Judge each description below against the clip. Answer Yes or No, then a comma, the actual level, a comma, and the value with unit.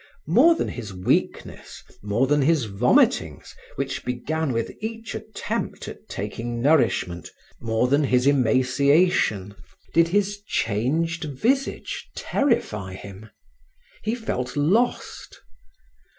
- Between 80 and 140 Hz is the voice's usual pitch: Yes, low, 135 Hz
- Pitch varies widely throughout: Yes, wide, 7.0 semitones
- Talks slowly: Yes, slow, 110 wpm